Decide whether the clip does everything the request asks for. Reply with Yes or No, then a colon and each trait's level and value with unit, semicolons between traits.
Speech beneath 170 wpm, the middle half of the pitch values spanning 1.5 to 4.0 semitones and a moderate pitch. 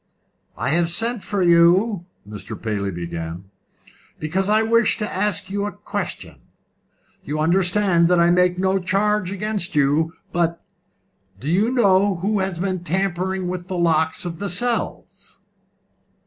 Yes: average, 145 wpm; average, 3.2 semitones; medium, 180 Hz